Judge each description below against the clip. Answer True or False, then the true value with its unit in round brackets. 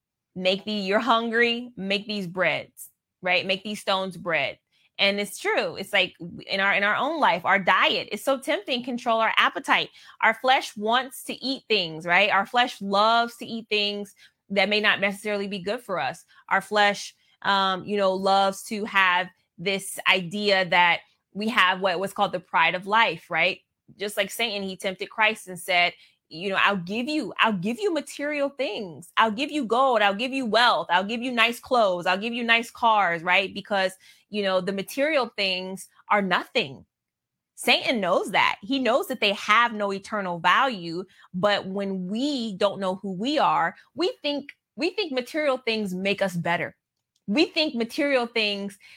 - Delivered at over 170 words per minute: True (185 wpm)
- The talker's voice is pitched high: True (205 Hz)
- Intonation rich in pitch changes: False (3.8 semitones)